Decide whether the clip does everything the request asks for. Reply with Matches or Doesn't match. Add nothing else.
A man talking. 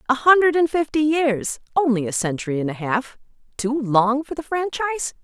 Doesn't match